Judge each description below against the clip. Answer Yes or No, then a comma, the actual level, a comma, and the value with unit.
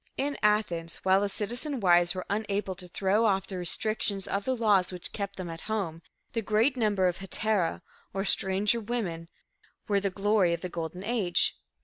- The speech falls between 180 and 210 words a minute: Yes, average, 185 wpm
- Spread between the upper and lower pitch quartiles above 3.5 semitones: No, average, 3.0 semitones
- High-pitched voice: Yes, high, 195 Hz